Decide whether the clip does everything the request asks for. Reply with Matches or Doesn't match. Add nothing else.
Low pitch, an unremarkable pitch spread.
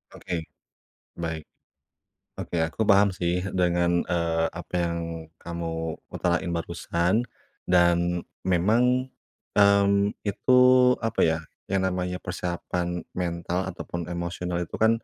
Doesn't match